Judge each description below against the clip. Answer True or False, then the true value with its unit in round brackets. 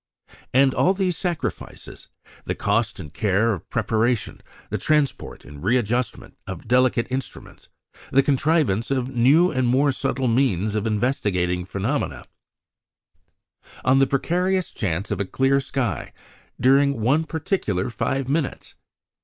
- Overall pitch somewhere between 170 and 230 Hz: False (125 Hz)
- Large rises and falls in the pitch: False (4.7 semitones)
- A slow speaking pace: True (130 wpm)